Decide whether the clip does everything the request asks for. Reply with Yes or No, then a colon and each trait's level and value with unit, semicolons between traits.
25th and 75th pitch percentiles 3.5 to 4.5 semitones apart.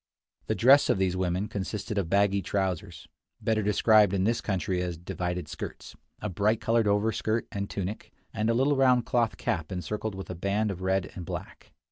No: average, 2.9 semitones